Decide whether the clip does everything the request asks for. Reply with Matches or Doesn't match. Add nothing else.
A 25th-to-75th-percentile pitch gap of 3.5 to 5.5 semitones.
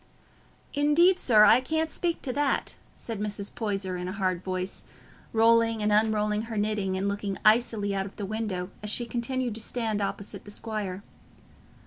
Doesn't match